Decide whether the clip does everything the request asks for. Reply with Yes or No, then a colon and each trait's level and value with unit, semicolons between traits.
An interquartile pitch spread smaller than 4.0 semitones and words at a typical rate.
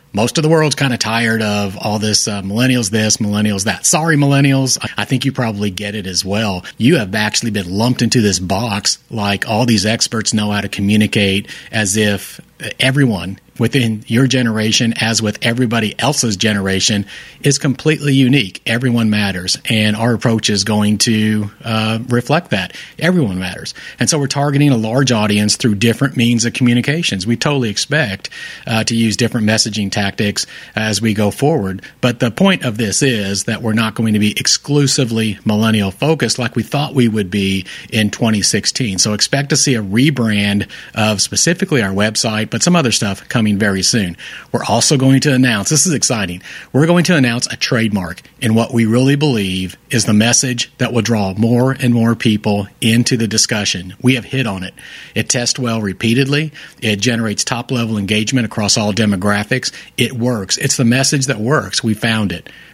Yes: average, 3.4 semitones; average, 185 wpm